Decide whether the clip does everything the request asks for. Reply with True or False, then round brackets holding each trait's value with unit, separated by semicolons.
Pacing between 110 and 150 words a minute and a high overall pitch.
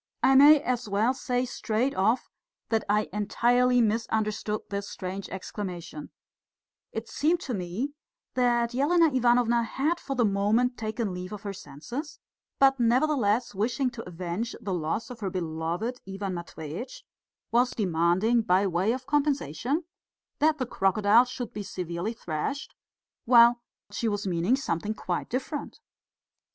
True (140 wpm; 225 Hz)